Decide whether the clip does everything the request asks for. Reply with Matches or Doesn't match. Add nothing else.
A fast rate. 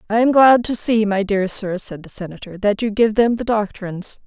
Matches